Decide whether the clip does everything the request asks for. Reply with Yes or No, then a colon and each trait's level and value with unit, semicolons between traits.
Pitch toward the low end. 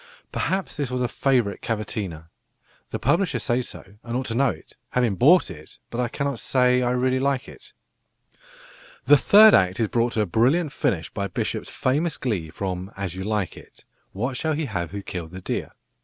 Yes: low, 120 Hz